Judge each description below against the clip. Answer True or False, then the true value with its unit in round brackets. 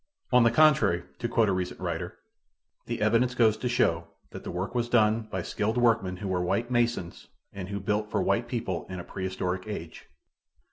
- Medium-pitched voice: False (105 Hz)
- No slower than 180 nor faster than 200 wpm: True (195 wpm)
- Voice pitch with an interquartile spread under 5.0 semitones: True (4.2 semitones)